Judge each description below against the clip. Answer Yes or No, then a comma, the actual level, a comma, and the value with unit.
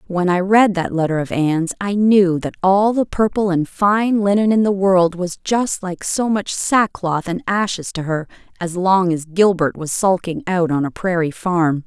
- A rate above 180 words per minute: Yes, average, 200 wpm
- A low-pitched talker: No, medium, 185 Hz